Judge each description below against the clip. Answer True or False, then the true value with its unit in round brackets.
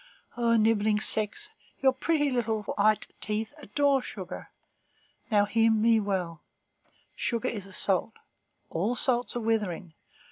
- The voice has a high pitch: True (220 Hz)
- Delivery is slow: True (130 wpm)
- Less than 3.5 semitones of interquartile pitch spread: True (2.9 semitones)